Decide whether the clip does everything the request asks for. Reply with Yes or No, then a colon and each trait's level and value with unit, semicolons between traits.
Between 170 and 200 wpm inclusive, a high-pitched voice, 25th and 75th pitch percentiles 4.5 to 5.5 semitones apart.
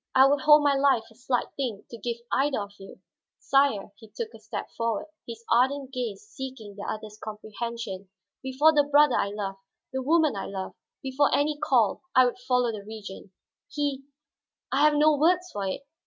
Yes: average, 185 wpm; very high, 250 Hz; average, 4.8 semitones